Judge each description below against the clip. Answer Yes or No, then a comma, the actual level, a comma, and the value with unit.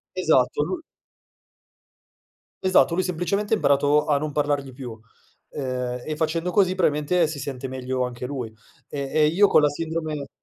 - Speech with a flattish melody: No, average, 3.8 semitones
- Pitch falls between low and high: Yes, medium, 150 Hz